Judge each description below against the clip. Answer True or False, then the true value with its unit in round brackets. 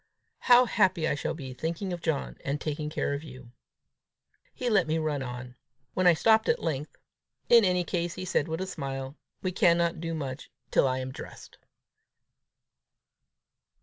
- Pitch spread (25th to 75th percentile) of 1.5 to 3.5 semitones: False (4.6 semitones)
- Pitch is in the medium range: True (160 Hz)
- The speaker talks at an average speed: True (170 wpm)